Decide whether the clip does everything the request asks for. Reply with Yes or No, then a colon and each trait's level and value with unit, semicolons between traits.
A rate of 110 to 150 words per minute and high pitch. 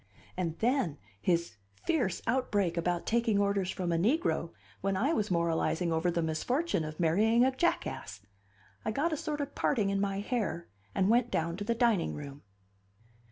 No: average, 170 wpm; high, 195 Hz